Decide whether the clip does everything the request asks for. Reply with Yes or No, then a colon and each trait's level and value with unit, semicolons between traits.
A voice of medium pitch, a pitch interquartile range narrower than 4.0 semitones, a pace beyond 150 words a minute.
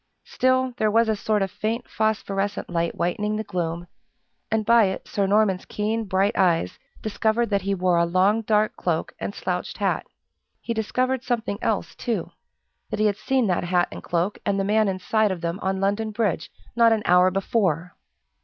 No: high, 205 Hz; average, 2.9 semitones; average, 185 wpm